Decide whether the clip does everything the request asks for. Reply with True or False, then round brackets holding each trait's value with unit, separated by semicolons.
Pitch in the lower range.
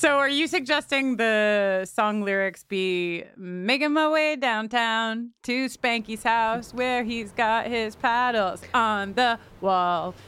False (230 Hz)